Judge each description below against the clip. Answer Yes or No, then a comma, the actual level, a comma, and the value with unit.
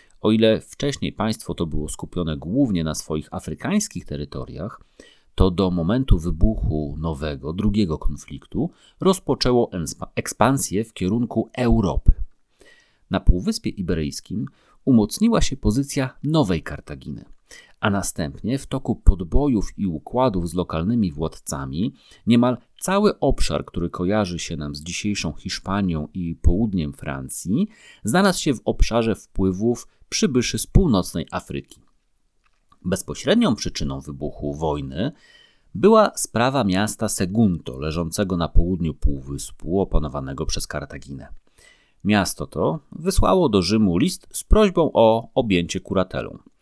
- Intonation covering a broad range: Yes, wide, 6.6 semitones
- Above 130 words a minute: No, average, 115 wpm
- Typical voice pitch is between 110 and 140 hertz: No, very low, 95 Hz